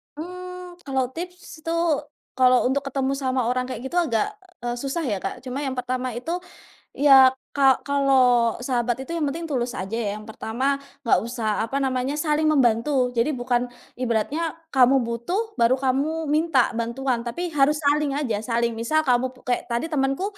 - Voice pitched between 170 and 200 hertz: No, very high, 265 Hz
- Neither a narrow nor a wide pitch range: Yes, average, 3.6 semitones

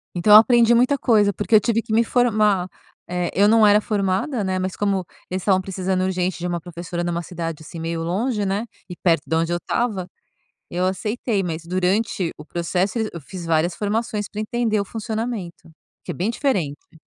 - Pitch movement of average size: Yes, average, 3.7 semitones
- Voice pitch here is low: No, high, 190 Hz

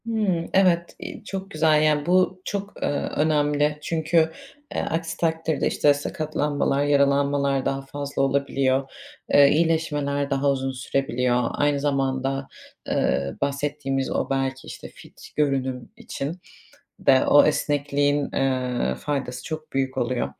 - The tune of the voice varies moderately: No, narrow, 2.3 semitones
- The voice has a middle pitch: Yes, medium, 145 Hz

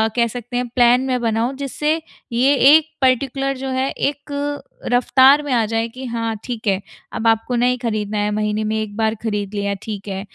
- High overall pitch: Yes, high, 235 Hz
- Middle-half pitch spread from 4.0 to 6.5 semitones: No, average, 3.4 semitones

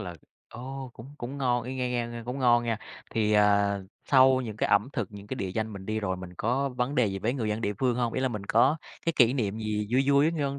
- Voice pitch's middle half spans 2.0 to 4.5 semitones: Yes, average, 3.6 semitones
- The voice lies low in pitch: Yes, low, 120 Hz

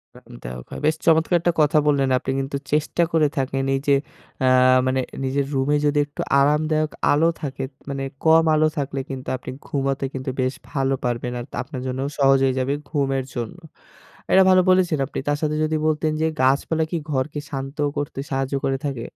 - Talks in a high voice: No, medium, 140 Hz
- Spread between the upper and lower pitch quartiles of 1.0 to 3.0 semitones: Yes, narrow, 2.5 semitones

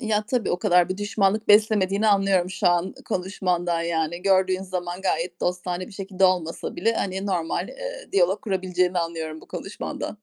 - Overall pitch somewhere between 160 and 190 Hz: Yes, medium, 185 Hz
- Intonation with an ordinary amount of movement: No, narrow, 2.3 semitones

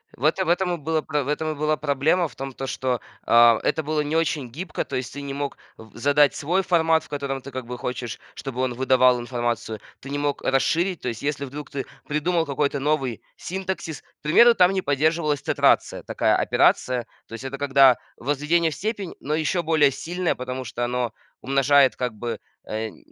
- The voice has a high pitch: No, medium, 140 Hz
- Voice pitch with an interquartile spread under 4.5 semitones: Yes, average, 3.8 semitones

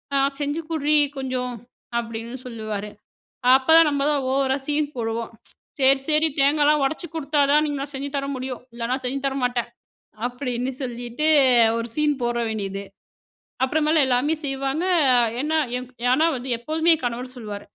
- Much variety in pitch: No, average, 3.7 semitones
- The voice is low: No, very high, 270 Hz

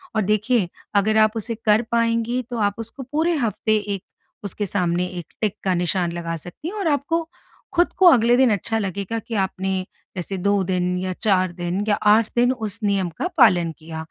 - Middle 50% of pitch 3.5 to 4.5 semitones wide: Yes, average, 3.9 semitones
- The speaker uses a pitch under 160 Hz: No, high, 205 Hz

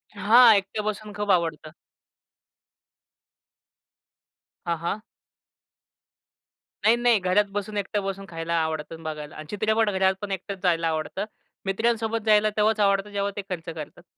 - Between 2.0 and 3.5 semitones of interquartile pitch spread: No, average, 3.9 semitones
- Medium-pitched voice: No, high, 200 Hz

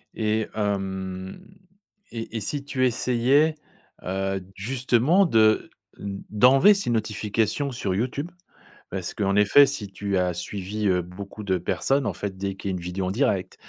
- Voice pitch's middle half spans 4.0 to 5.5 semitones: Yes, average, 4.7 semitones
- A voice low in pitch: Yes, low, 105 Hz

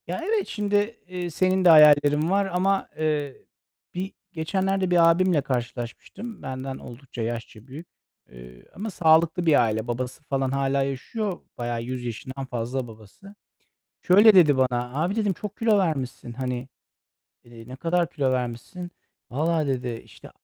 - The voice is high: No, medium, 145 Hz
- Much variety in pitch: Yes, wide, 6.4 semitones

